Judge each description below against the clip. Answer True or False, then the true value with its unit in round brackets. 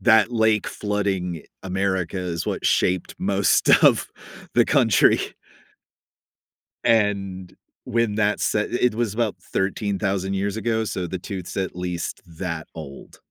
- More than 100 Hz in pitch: False (95 Hz)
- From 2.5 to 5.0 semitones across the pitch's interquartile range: True (2.9 semitones)